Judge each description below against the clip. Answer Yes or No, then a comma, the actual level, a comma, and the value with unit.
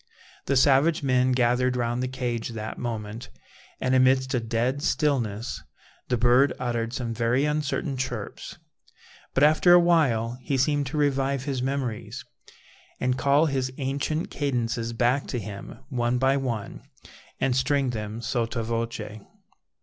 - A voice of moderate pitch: No, low, 125 Hz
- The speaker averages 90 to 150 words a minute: Yes, average, 140 wpm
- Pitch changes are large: No, average, 2.8 semitones